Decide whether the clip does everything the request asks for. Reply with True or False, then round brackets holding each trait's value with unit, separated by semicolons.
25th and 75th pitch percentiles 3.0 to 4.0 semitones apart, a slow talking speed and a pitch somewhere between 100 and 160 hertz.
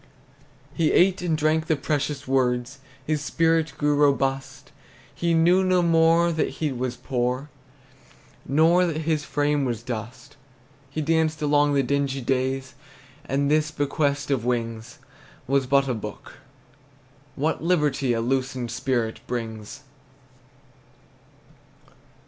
True (3.4 semitones; 125 wpm; 140 Hz)